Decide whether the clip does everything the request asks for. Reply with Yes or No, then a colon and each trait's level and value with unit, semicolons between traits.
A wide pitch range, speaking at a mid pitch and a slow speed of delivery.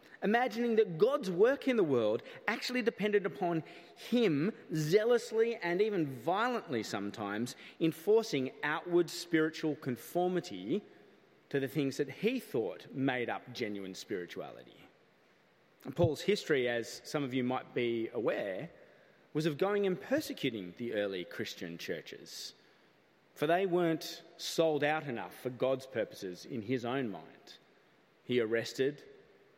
Yes: wide, 8.2 semitones; medium, 160 Hz; slow, 130 wpm